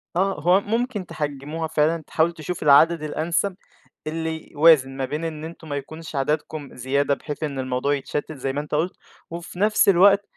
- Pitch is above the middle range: No, medium, 155 Hz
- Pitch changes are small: No, average, 3.1 semitones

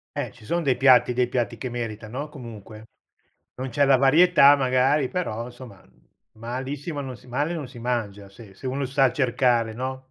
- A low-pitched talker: Yes, low, 130 Hz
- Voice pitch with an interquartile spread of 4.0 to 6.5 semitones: No, average, 2.8 semitones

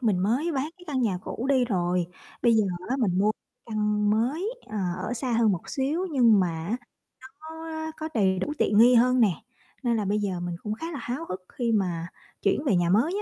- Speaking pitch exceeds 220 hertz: Yes, high, 230 Hz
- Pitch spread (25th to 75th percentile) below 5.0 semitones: No, average, 5.3 semitones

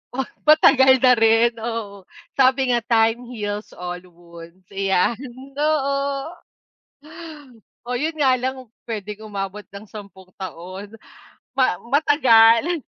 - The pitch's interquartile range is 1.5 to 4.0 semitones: No, average, 4.9 semitones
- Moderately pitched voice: No, high, 225 Hz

